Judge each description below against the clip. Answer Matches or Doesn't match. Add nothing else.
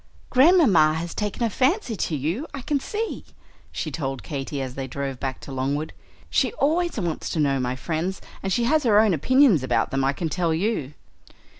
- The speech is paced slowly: Doesn't match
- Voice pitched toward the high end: Doesn't match